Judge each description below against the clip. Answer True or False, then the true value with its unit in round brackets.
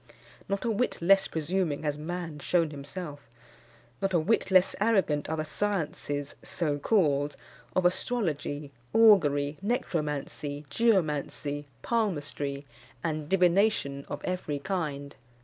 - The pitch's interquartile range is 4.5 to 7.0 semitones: True (4.9 semitones)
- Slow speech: True (115 wpm)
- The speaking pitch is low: False (160 Hz)